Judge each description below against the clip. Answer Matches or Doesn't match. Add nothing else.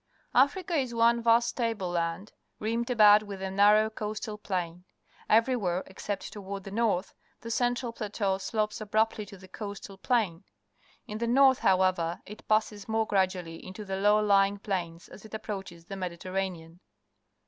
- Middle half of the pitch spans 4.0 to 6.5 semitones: Doesn't match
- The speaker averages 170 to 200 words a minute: Doesn't match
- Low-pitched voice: Doesn't match